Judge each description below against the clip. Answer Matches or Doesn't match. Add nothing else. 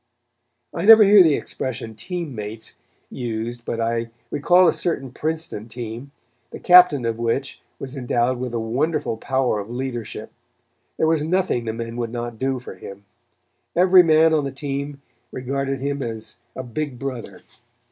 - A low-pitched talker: Matches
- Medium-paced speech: Matches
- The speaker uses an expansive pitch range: Doesn't match